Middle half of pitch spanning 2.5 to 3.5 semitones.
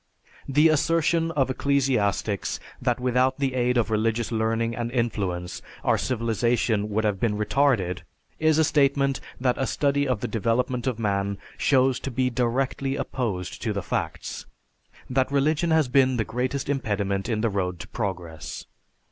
No: average, 4.1 semitones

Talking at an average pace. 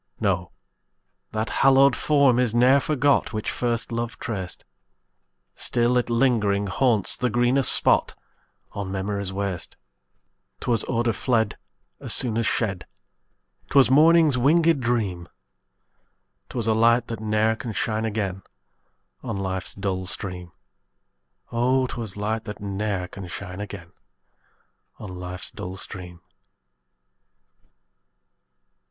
No: slow, 115 wpm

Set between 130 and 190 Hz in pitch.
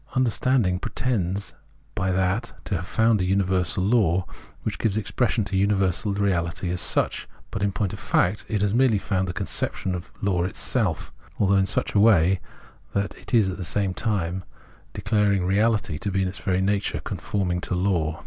No: very low, 95 Hz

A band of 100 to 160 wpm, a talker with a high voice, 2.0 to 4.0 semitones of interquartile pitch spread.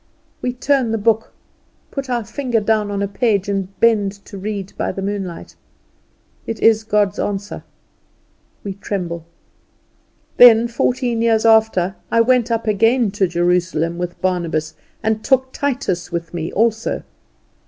Yes: average, 145 wpm; high, 210 Hz; average, 3.5 semitones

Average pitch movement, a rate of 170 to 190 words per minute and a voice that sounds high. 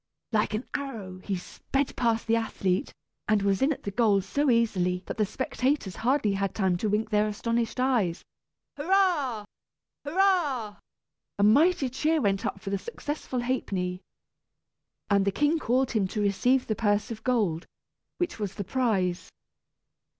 No: average, 4.9 semitones; average, 155 wpm; high, 220 Hz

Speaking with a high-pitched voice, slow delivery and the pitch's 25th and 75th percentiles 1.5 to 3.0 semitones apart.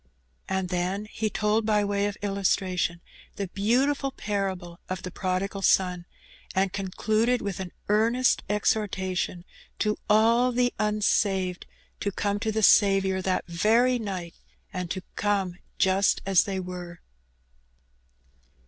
Yes: high, 195 Hz; slow, 130 wpm; narrow, 2.5 semitones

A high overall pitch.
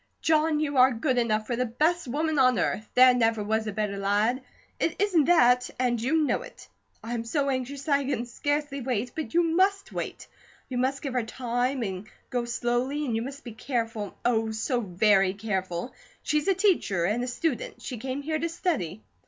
Yes: very high, 250 Hz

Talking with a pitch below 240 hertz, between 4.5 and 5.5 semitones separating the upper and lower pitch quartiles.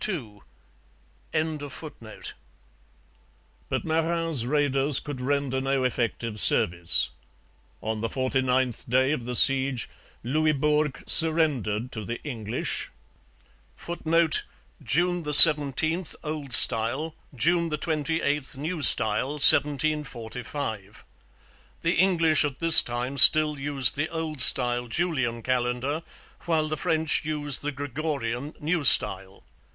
No: medium, 140 Hz; average, 4.1 semitones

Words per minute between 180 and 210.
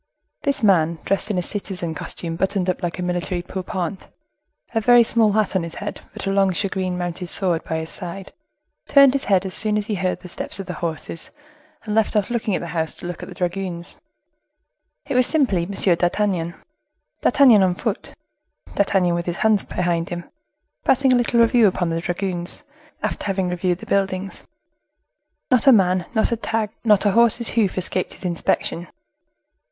Yes: average, 190 wpm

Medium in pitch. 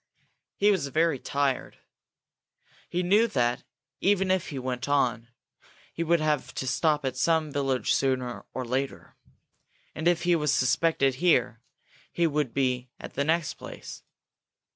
Yes: medium, 145 Hz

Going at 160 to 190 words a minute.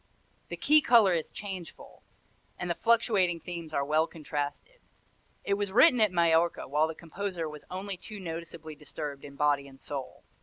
Yes: average, 165 wpm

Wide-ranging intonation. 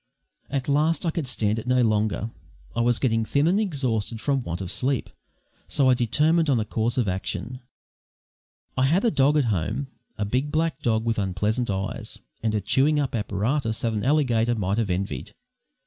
No: average, 4.7 semitones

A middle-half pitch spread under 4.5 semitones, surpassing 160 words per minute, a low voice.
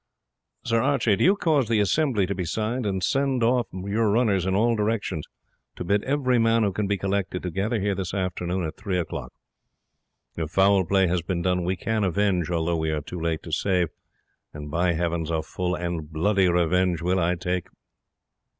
Yes: average, 3.6 semitones; average, 200 wpm; very low, 95 Hz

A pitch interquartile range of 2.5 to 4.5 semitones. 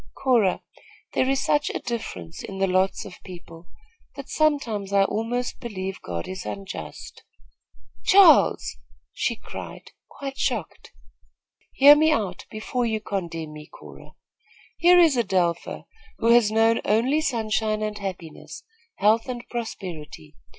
No: average, 4.9 semitones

